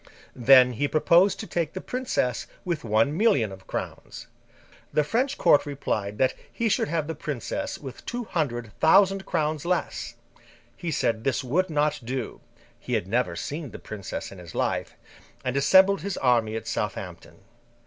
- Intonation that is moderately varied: No, wide, 6.9 semitones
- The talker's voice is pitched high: No, medium, 145 Hz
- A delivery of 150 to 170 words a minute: Yes, average, 165 wpm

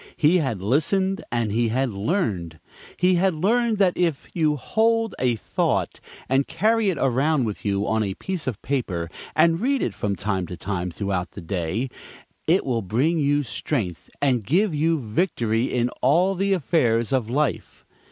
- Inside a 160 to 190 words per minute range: Yes, average, 170 wpm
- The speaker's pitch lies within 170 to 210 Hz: No, low, 135 Hz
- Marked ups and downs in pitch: Yes, wide, 8.3 semitones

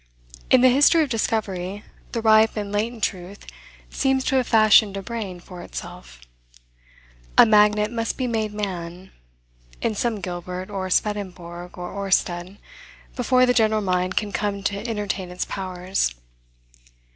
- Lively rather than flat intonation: No, average, 3.4 semitones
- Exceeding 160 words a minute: No, average, 145 wpm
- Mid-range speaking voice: No, high, 205 Hz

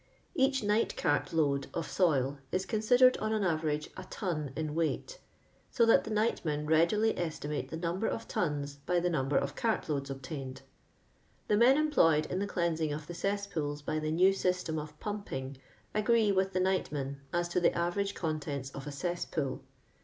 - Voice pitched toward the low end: No, medium, 170 Hz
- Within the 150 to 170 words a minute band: No, average, 185 wpm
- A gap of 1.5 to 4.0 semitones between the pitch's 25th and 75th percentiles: No, average, 5.3 semitones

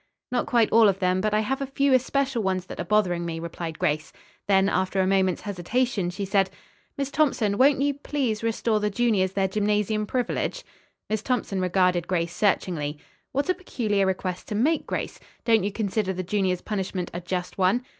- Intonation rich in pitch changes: No, average, 4.1 semitones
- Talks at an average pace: Yes, average, 190 wpm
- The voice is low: No, high, 200 Hz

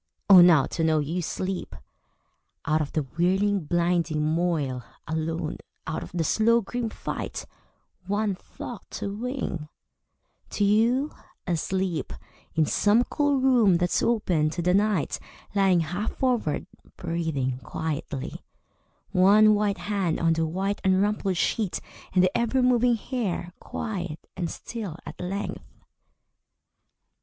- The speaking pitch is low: No, medium, 185 Hz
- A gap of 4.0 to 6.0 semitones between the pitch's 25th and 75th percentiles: Yes, average, 4.6 semitones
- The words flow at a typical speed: No, slow, 130 wpm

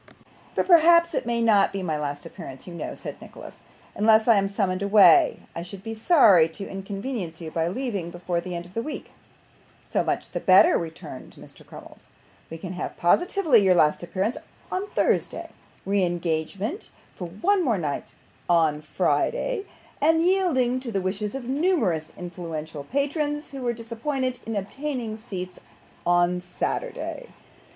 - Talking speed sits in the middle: Yes, average, 160 wpm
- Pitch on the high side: Yes, high, 200 Hz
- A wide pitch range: Yes, wide, 7.5 semitones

